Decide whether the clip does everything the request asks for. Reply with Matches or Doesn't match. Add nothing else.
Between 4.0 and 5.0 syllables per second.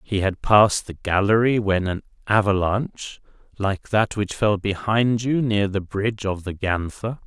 Matches